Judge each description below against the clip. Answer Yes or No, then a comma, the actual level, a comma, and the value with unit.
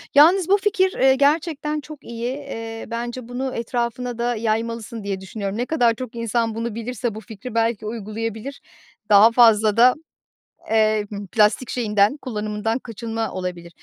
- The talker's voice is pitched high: Yes, high, 230 Hz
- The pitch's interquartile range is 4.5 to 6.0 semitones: No, narrow, 2.6 semitones